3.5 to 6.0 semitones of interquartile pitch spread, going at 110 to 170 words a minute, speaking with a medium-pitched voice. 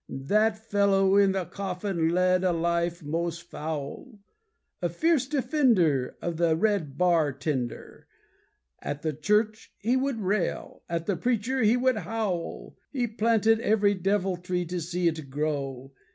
Yes: average, 4.7 semitones; average, 140 wpm; medium, 180 Hz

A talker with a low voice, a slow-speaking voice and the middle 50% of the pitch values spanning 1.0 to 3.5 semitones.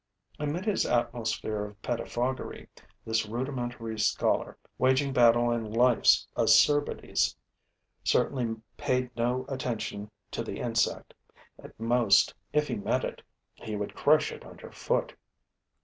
Yes: low, 120 Hz; slow, 120 wpm; average, 2.7 semitones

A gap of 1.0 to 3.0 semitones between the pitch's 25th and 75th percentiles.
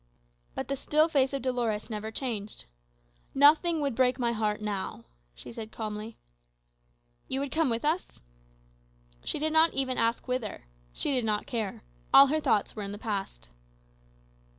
No: average, 4.6 semitones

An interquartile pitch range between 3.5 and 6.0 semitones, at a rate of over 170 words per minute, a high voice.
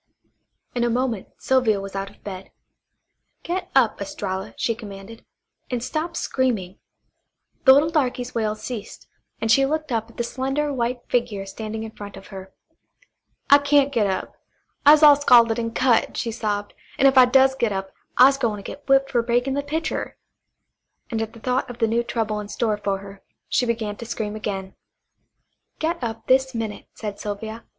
Yes: average, 4.0 semitones; average, 180 wpm; high, 235 Hz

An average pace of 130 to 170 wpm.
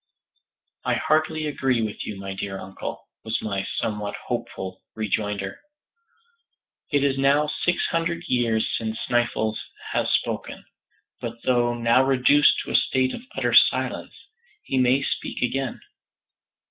Yes: slow, 135 wpm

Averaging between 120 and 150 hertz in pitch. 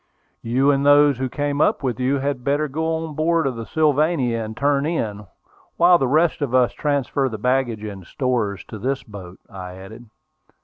Yes: low, 135 Hz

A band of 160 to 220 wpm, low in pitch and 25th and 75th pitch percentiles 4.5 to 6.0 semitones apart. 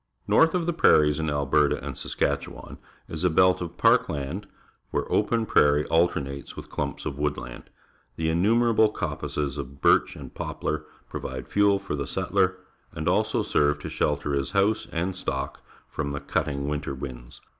Yes: average, 170 wpm; very low, 80 Hz; wide, 5.4 semitones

